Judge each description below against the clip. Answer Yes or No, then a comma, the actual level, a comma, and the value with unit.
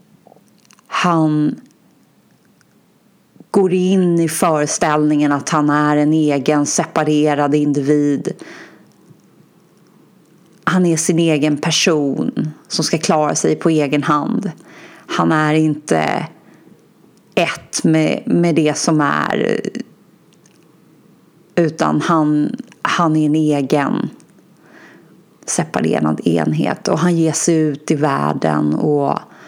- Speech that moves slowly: Yes, slow, 100 wpm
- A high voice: No, medium, 155 Hz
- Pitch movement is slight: Yes, narrow, 2.2 semitones